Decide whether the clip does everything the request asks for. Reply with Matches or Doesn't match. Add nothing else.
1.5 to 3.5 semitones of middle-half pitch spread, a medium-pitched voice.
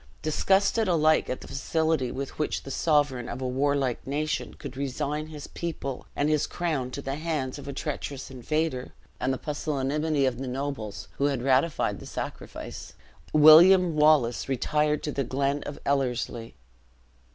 Matches